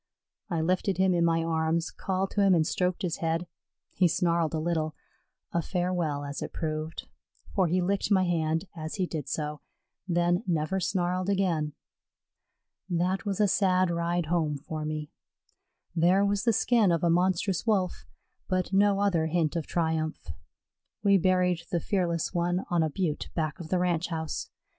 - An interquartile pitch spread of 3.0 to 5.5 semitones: No, narrow, 2.6 semitones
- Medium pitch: Yes, medium, 175 Hz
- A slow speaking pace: No, average, 170 wpm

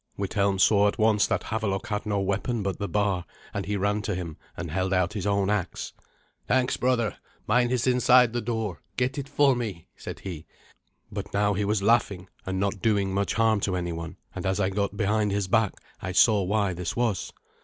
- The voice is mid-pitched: No, low, 100 Hz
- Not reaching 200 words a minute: No, fast, 205 wpm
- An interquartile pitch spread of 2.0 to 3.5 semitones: Yes, average, 2.8 semitones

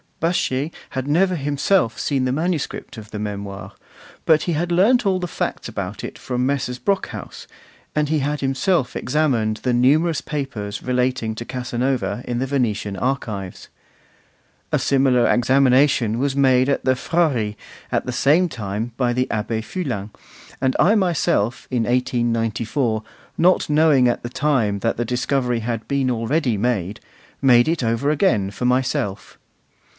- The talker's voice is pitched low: Yes, low, 125 Hz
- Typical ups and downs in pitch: Yes, average, 4.0 semitones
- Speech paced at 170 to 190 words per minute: No, average, 155 wpm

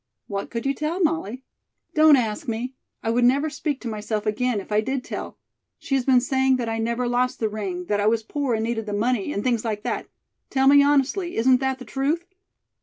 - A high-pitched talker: Yes, very high, 250 Hz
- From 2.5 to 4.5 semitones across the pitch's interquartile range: Yes, average, 3.7 semitones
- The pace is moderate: No, fast, 225 wpm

